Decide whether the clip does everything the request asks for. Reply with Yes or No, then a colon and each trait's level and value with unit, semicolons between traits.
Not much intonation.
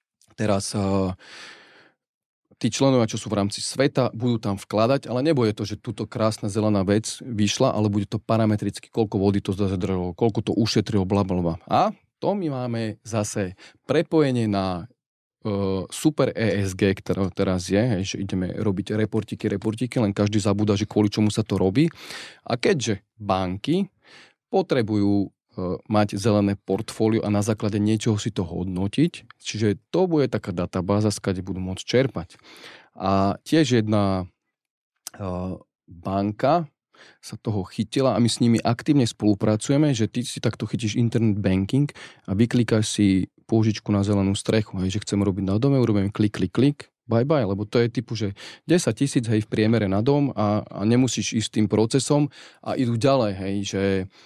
No: average, 3.2 semitones